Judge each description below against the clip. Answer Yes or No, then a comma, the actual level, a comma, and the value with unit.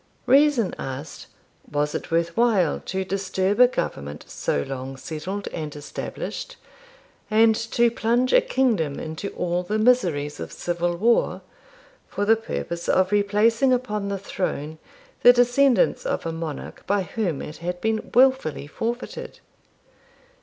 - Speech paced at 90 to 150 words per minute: Yes, average, 140 wpm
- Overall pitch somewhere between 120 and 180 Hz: No, high, 200 Hz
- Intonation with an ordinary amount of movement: No, wide, 6.3 semitones